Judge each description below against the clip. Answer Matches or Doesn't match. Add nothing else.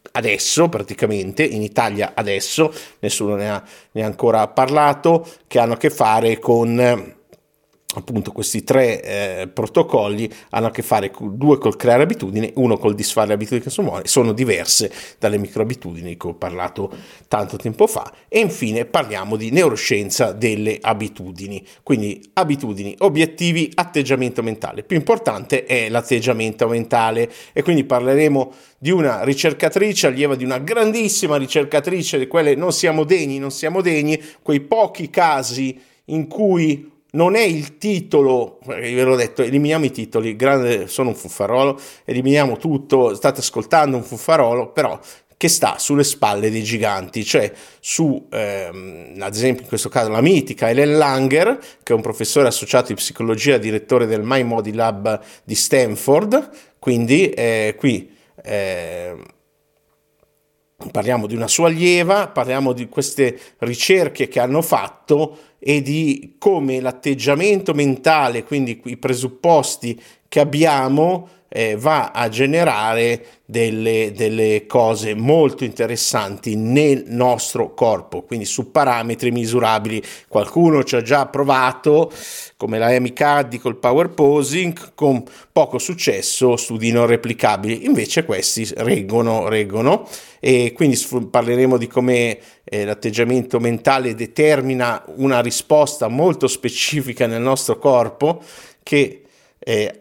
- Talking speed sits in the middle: Matches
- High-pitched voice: Doesn't match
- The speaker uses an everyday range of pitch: Matches